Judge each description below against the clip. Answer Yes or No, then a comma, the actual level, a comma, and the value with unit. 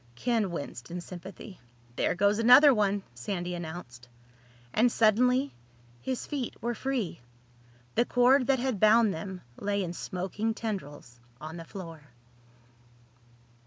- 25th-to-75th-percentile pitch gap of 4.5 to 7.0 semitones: Yes, wide, 5.5 semitones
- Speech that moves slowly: Yes, slow, 125 wpm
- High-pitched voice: Yes, high, 200 Hz